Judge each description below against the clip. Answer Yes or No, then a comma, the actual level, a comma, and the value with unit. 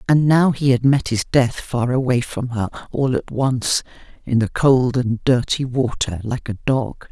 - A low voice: Yes, low, 125 Hz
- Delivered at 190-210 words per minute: Yes, average, 195 wpm